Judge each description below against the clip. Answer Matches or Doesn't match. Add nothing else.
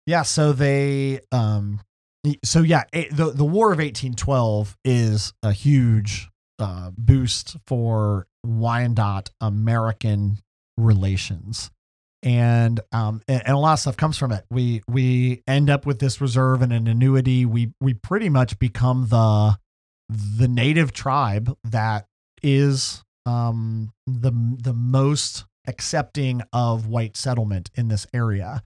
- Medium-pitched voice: Doesn't match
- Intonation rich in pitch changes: Doesn't match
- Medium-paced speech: Doesn't match